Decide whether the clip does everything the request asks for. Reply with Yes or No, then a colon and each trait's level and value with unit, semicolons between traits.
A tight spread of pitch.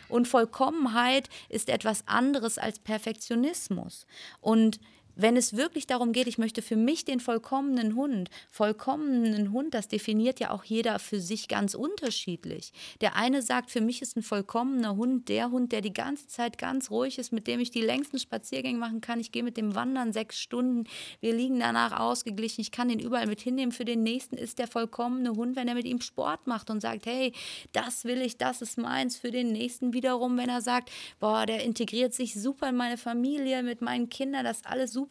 Yes: narrow, 2.2 semitones